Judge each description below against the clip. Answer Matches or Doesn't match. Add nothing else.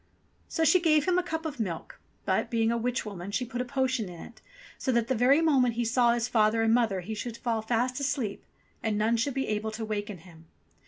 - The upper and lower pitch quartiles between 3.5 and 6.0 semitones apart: Doesn't match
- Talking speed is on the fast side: Matches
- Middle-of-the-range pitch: Doesn't match